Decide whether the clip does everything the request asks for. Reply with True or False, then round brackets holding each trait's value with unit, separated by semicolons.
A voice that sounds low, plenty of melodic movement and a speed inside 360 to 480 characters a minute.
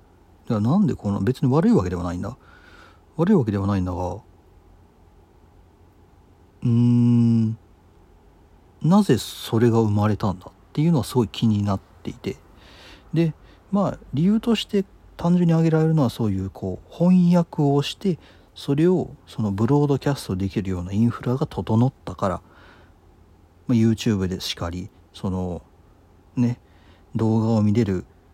False (105 Hz; 6.4 semitones; 290 characters per minute)